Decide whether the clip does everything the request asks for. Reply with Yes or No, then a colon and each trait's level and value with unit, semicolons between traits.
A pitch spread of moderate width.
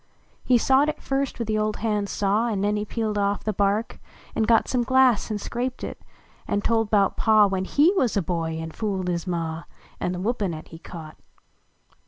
Yes: average, 3.6 semitones